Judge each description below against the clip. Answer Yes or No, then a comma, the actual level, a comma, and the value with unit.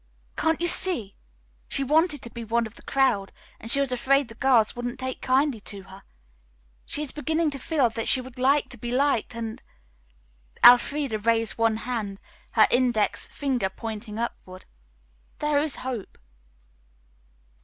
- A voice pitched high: Yes, high, 245 Hz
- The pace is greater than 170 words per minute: No, average, 160 wpm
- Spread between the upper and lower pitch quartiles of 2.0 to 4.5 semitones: Yes, average, 3.7 semitones